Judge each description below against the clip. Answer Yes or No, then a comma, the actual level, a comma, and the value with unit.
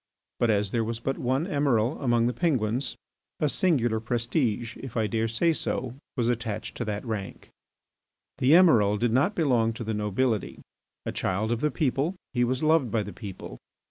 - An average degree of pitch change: Yes, average, 3.5 semitones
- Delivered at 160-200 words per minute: Yes, average, 180 wpm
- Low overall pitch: Yes, low, 120 Hz